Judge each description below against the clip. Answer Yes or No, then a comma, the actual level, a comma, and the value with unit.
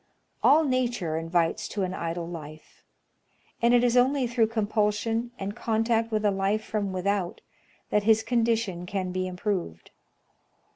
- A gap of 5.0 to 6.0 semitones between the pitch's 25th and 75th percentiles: No, average, 3.8 semitones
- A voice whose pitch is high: Yes, high, 210 Hz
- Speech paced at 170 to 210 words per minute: No, average, 145 wpm